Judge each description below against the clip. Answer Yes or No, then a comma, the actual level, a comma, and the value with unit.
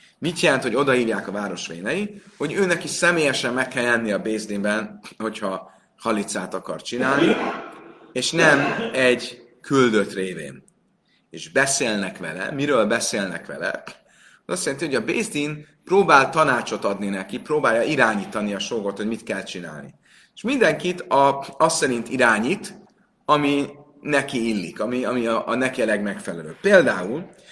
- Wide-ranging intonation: Yes, wide, 6.0 semitones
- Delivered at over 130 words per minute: Yes, average, 145 wpm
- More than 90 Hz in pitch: Yes, low, 130 Hz